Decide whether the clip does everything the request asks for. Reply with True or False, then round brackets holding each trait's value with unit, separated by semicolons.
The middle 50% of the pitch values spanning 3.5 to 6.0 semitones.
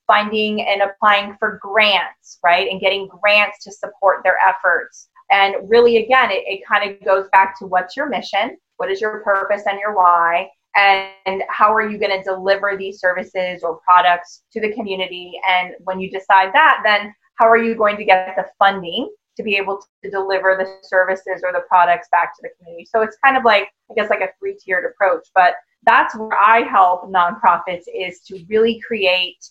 False (2.7 semitones)